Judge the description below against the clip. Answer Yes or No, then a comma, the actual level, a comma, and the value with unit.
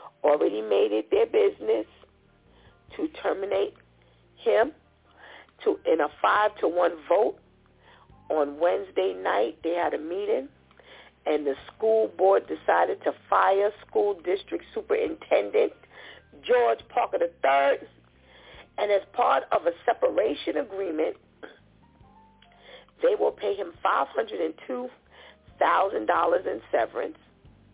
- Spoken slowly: Yes, slow, 105 wpm